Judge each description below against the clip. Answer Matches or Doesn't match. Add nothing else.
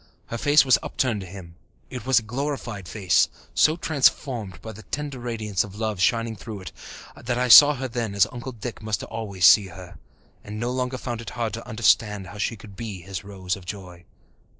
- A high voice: Doesn't match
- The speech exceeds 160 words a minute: Matches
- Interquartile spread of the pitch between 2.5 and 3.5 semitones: Doesn't match